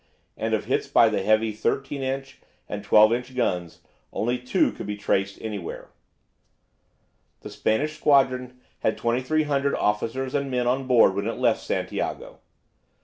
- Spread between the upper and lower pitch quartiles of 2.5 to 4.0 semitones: Yes, average, 3.7 semitones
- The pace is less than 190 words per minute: Yes, average, 145 wpm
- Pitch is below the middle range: Yes, low, 125 Hz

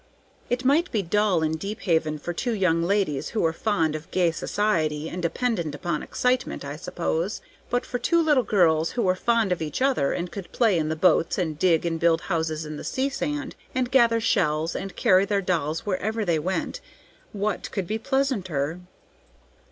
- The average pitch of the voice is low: No, medium, 185 Hz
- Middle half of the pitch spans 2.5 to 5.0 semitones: No, wide, 5.6 semitones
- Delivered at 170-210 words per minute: Yes, average, 190 wpm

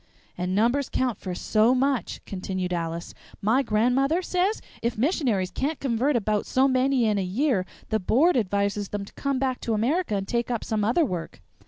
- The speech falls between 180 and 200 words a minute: Yes, average, 185 wpm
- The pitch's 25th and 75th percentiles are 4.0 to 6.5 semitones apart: Yes, average, 5.1 semitones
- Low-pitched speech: No, high, 230 Hz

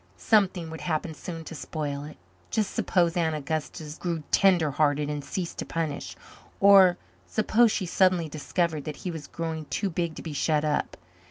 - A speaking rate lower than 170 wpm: No, average, 175 wpm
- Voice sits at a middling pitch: Yes, medium, 165 Hz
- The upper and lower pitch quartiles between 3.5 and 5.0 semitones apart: No, average, 2.9 semitones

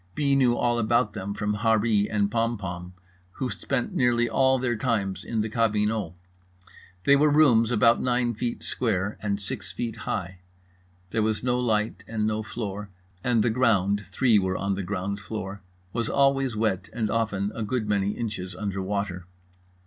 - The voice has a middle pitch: No, low, 110 Hz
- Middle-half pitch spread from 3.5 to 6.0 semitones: No, average, 2.9 semitones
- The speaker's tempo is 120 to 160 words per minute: No, average, 170 wpm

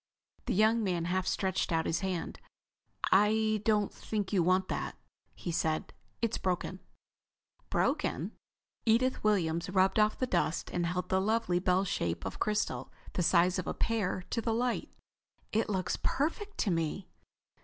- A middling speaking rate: Yes, average, 155 wpm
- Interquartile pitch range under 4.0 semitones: Yes, average, 3.5 semitones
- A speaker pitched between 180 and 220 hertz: Yes, high, 190 Hz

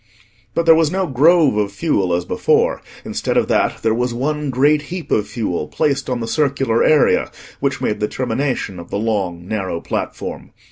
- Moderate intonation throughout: No, wide, 6.2 semitones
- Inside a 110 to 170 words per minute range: No, average, 185 wpm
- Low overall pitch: Yes, low, 125 Hz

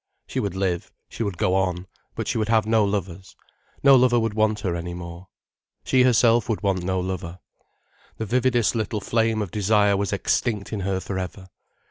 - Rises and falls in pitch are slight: No, average, 3.1 semitones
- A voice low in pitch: Yes, low, 100 Hz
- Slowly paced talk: No, average, 190 wpm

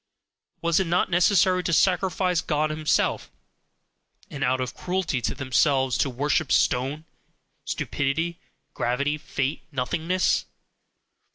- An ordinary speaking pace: No, slow, 110 wpm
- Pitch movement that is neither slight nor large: Yes, average, 4.4 semitones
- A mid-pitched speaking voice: Yes, medium, 155 Hz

